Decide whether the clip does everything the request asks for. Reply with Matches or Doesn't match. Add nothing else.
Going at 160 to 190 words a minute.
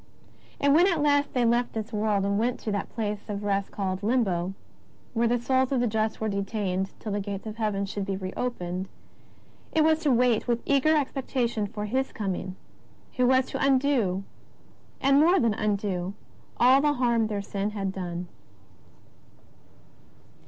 Matches